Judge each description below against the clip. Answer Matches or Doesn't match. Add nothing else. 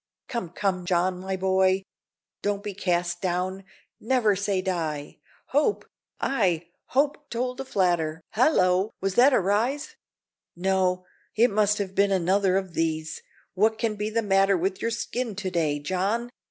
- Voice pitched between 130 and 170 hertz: Doesn't match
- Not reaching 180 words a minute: Matches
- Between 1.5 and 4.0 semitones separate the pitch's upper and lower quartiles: Matches